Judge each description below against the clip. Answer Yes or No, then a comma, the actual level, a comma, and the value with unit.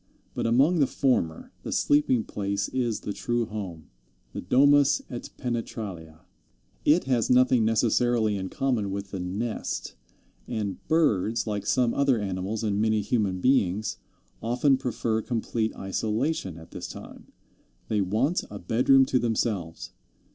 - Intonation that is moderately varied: Yes, average, 4.0 semitones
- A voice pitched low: Yes, low, 110 Hz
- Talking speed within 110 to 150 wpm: Yes, average, 140 wpm